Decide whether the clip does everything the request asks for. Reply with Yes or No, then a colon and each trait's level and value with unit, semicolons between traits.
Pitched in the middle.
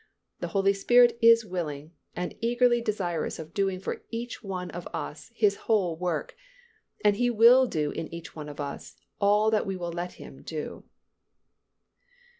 No: high, 195 Hz